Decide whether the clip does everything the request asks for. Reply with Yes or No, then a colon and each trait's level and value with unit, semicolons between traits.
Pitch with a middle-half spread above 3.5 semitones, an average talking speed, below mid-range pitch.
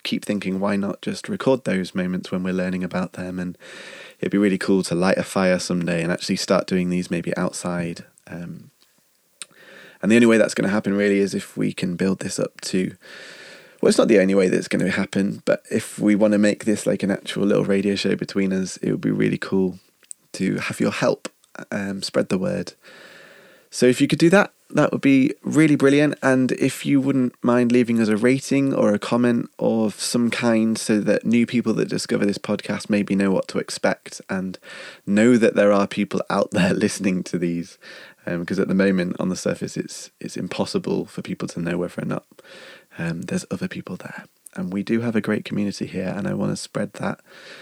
No: average, 4.3 semitones; fast, 220 wpm; low, 100 Hz